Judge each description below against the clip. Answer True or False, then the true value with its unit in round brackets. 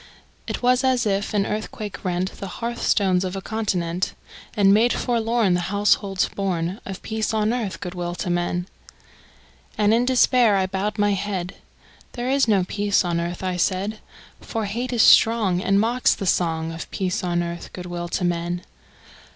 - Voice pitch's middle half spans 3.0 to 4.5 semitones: True (3.6 semitones)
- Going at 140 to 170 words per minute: False (180 wpm)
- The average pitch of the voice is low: False (195 Hz)